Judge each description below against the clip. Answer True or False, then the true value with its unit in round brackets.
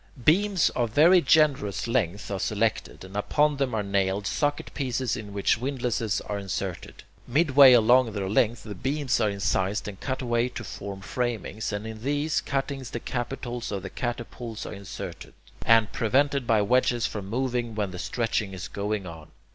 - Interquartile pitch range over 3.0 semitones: True (4.3 semitones)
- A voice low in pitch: True (115 Hz)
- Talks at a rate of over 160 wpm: True (170 wpm)